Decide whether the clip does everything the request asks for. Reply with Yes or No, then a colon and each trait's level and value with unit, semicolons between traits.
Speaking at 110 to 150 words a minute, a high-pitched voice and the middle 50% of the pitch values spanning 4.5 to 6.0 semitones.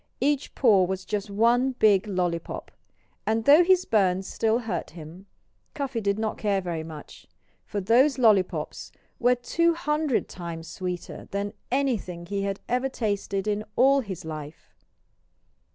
Yes: average, 145 wpm; high, 210 Hz; average, 5.2 semitones